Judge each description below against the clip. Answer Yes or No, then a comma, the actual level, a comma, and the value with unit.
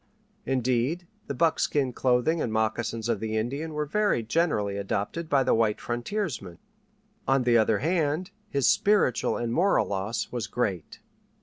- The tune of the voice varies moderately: No, wide, 5.9 semitones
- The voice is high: No, low, 125 Hz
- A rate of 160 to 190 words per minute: No, average, 145 wpm